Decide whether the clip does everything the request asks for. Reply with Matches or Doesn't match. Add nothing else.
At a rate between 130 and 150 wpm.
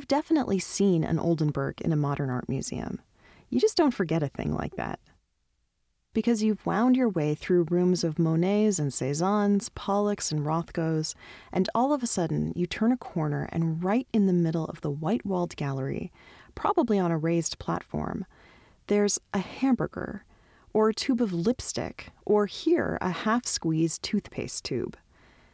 Doesn't match